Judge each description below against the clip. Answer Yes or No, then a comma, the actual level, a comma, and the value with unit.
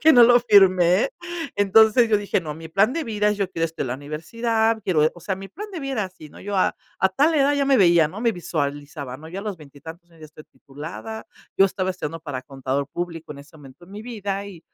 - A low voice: No, medium, 185 Hz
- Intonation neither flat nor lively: No, wide, 5.9 semitones